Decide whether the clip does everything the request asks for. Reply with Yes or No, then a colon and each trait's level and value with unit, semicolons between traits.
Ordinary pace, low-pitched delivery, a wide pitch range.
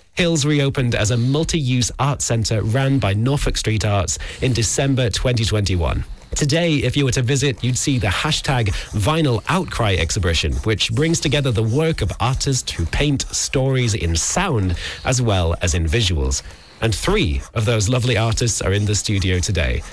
Yes: average, 170 wpm; low, 115 Hz; wide, 6.1 semitones